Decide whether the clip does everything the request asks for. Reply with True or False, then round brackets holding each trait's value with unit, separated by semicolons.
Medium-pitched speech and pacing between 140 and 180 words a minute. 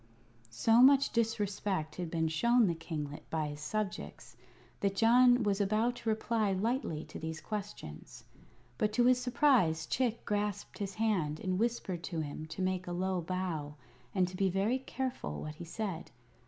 False (195 Hz; 170 wpm)